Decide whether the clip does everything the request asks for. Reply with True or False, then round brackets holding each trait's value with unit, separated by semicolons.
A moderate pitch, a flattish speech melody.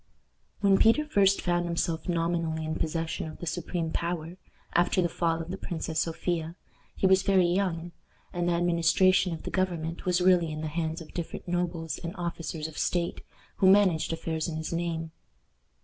True (170 Hz; 1.6 semitones)